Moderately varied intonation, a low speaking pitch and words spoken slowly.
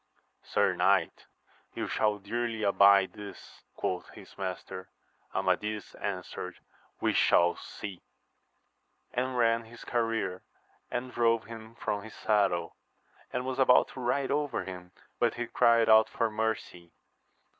Yes: average, 3.2 semitones; low, 110 Hz; slow, 130 wpm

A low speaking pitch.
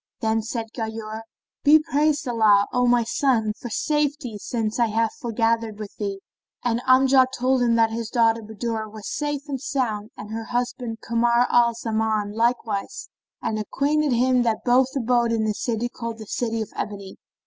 No: high, 230 Hz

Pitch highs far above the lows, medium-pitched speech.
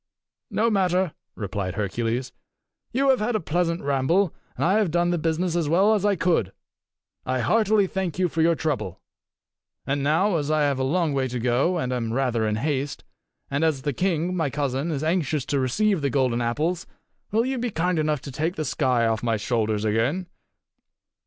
Yes: wide, 5.9 semitones; medium, 155 Hz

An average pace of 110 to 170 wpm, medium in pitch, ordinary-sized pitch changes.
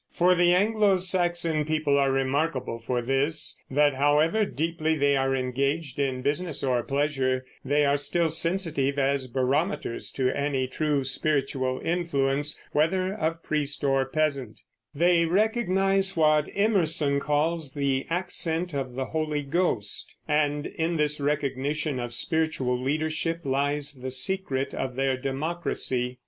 Yes: slow, 135 wpm; medium, 145 Hz; average, 3.5 semitones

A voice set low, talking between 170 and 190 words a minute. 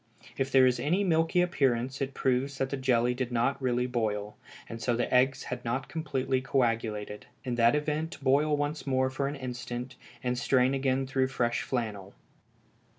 Yes: low, 130 Hz; average, 175 wpm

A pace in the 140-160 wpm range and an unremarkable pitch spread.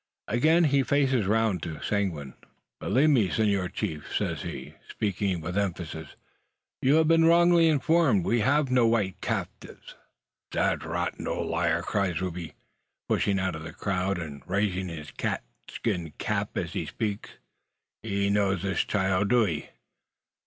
No: average, 155 wpm; wide, 5.7 semitones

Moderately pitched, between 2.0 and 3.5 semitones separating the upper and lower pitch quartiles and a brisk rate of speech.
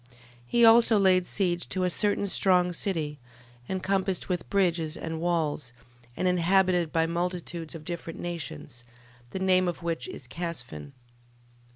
No: medium, 175 Hz; narrow, 2.4 semitones; average, 145 wpm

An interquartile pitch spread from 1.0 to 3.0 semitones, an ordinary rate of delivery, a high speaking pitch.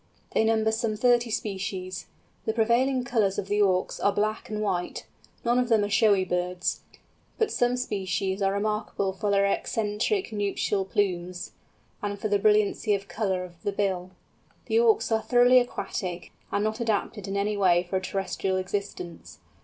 Yes: narrow, 2.6 semitones; average, 170 wpm; high, 205 Hz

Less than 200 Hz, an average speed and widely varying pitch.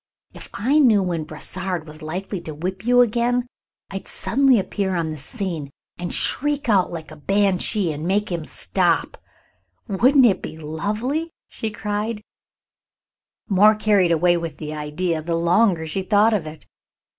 No: high, 190 Hz; average, 155 wpm; average, 4.9 semitones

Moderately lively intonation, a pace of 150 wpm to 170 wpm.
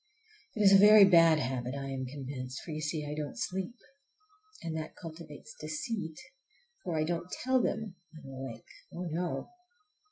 Yes: average, 4.8 semitones; average, 160 wpm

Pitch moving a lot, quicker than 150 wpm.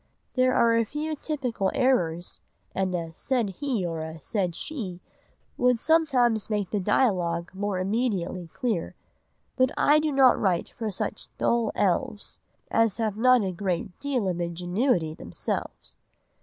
No: wide, 6.0 semitones; average, 145 wpm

